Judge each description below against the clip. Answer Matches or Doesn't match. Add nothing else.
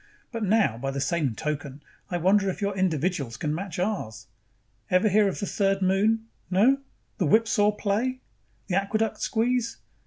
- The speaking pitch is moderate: Doesn't match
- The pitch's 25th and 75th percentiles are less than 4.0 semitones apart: Doesn't match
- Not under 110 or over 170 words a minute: Matches